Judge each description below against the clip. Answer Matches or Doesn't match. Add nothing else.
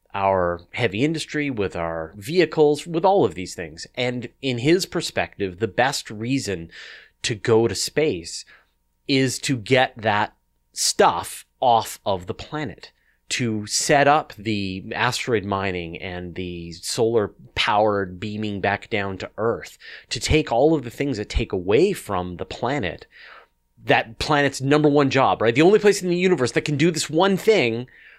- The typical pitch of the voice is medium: Doesn't match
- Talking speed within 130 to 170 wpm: Matches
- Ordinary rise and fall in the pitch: Doesn't match